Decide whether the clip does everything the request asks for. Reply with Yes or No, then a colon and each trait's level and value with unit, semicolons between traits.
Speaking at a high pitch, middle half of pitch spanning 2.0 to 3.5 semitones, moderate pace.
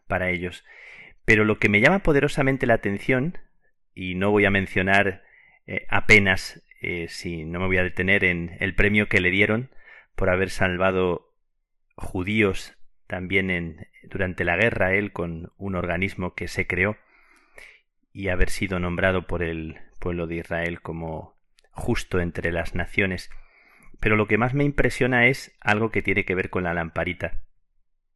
No: very low, 95 Hz; average, 3.0 semitones; average, 160 wpm